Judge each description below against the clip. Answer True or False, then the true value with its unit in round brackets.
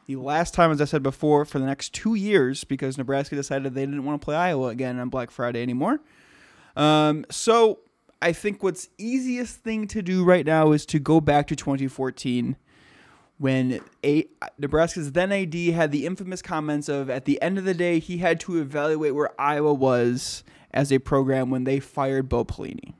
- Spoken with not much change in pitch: False (4.1 semitones)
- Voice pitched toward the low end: False (150 Hz)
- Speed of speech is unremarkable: True (190 wpm)